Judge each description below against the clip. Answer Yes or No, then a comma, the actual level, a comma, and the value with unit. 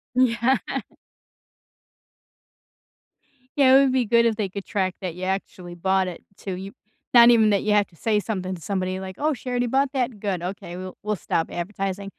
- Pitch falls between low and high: No, high, 200 Hz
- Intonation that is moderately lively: Yes, average, 4.1 semitones